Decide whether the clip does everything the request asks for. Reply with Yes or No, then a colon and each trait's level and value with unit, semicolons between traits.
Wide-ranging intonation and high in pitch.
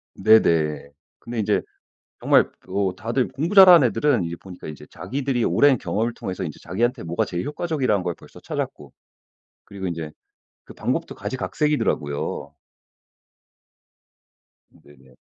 No: wide, 7.4 semitones; low, 105 Hz